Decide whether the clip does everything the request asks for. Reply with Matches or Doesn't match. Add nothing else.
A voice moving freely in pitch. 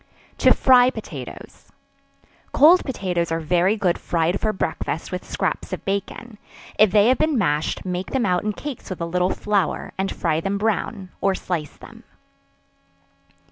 Doesn't match